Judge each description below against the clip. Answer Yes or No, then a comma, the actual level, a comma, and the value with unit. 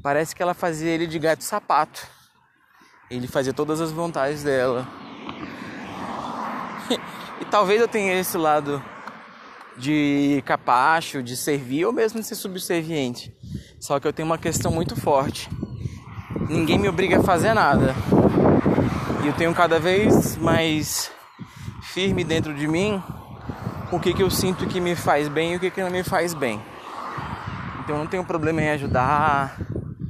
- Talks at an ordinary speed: Yes, average, 155 wpm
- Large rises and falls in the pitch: No, average, 4.3 semitones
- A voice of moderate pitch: Yes, medium, 160 Hz